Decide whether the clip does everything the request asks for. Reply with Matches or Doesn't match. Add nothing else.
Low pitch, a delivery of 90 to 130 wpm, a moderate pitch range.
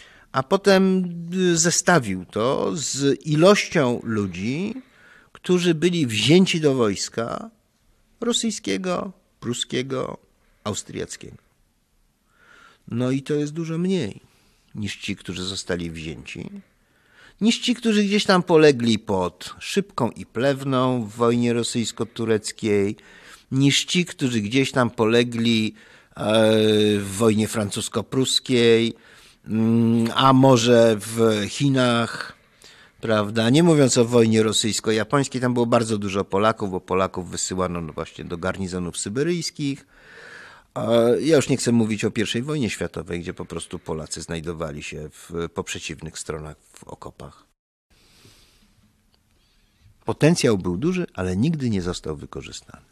Doesn't match